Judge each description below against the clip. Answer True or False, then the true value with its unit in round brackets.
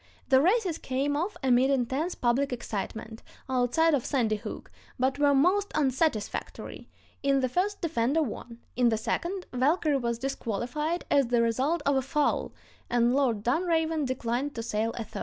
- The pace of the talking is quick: False (160 wpm)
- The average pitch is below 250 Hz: False (265 Hz)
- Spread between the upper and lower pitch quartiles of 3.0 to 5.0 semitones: True (4.5 semitones)